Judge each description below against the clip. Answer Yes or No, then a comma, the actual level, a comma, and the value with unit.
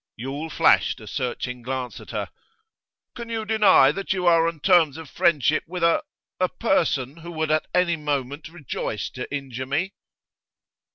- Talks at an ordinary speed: Yes, average, 165 wpm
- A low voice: No, medium, 155 Hz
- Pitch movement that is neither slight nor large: Yes, average, 4.5 semitones